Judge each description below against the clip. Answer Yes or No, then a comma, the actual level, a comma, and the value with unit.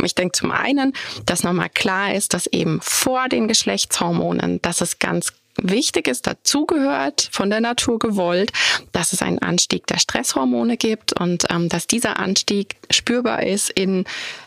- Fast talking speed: No, average, 160 wpm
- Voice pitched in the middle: No, high, 210 Hz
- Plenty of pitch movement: Yes, wide, 5.7 semitones